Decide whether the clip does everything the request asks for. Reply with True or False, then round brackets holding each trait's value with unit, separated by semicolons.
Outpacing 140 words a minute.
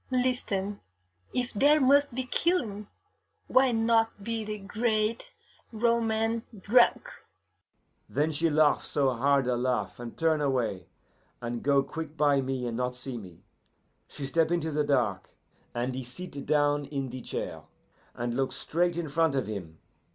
True (150 wpm)